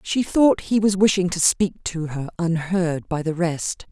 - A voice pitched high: No, medium, 175 Hz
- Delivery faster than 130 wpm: Yes, average, 200 wpm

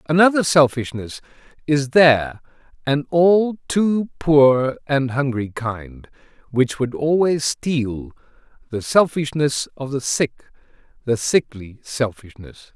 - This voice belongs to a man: Yes, male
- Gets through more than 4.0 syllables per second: No, 3.7 syllables/s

